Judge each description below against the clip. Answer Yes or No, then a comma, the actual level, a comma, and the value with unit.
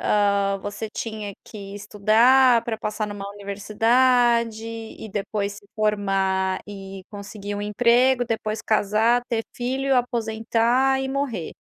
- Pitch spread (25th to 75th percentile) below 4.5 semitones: Yes, average, 2.8 semitones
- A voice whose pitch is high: Yes, high, 215 Hz